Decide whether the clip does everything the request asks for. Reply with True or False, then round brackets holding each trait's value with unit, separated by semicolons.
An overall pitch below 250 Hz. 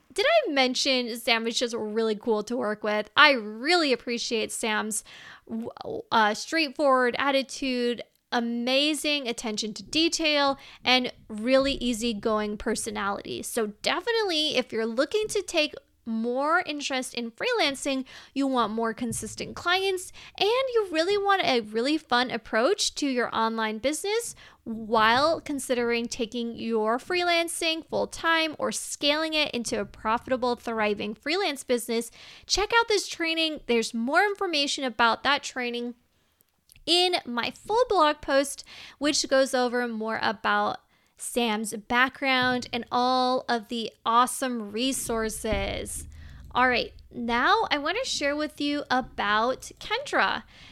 False (255 Hz)